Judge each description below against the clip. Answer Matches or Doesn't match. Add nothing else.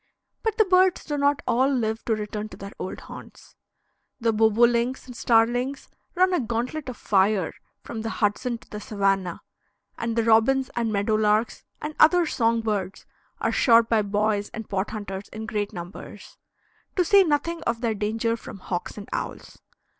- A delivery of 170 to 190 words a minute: Matches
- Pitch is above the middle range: Matches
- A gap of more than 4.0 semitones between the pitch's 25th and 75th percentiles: Doesn't match